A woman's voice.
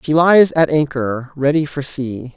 No: male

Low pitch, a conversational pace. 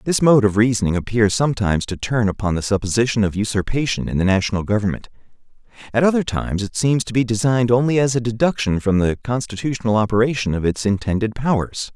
Yes: low, 115 Hz; average, 185 wpm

